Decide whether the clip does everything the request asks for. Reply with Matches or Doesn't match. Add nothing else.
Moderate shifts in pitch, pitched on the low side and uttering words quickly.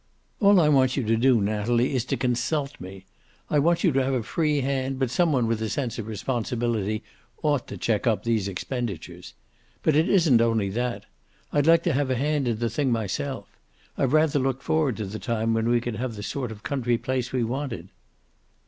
Matches